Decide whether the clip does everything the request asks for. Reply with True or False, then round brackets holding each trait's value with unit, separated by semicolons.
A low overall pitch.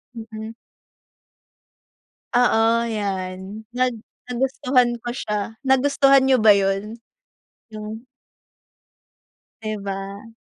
False (220 Hz)